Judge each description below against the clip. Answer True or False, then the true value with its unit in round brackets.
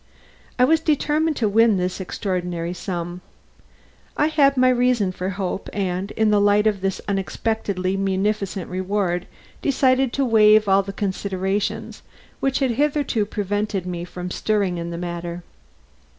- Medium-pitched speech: False (200 Hz)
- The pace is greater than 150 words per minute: False (145 wpm)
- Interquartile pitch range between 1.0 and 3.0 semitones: False (3.9 semitones)